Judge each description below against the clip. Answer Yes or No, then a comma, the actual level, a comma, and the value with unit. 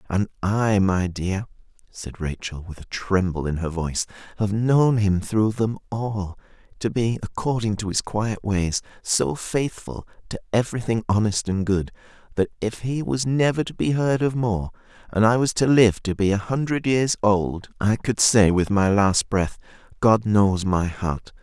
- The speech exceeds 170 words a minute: Yes, average, 180 wpm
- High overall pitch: No, low, 105 Hz